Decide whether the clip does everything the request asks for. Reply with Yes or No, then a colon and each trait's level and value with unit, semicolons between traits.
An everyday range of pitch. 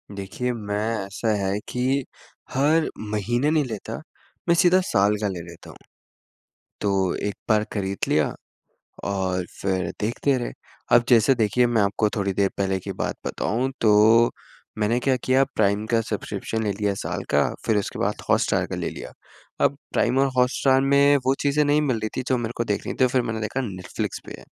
Yes: average, 4.3 semitones